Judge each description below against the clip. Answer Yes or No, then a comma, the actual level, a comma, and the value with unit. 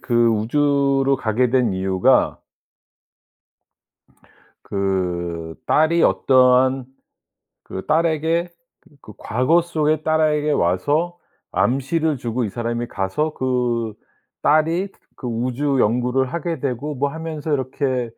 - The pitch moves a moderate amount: Yes, average, 4.6 semitones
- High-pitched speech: No, low, 130 Hz